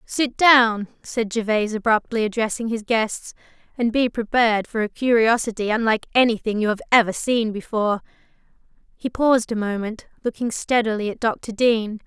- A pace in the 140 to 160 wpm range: Yes, average, 150 wpm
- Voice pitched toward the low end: No, high, 225 Hz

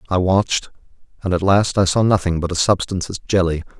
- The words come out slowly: No, fast, 205 wpm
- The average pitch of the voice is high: No, very low, 90 Hz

